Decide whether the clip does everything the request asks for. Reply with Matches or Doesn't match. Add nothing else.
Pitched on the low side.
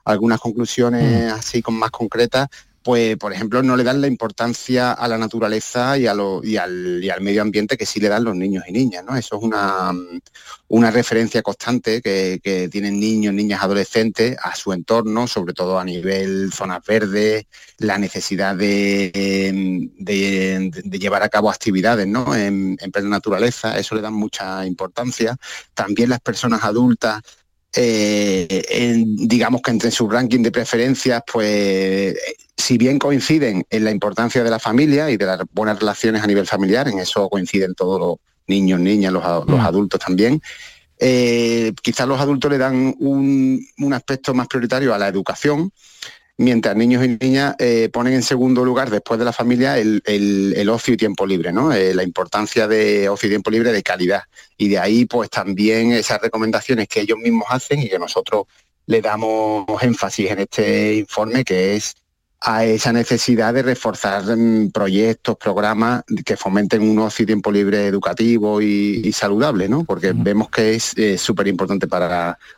Matches